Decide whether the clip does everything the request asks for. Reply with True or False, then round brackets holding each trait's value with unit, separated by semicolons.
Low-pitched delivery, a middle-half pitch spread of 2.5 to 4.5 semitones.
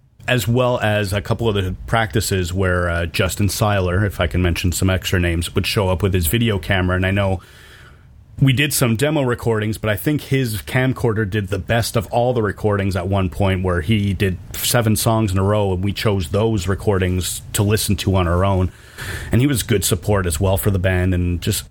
True (105 Hz; 3.3 semitones)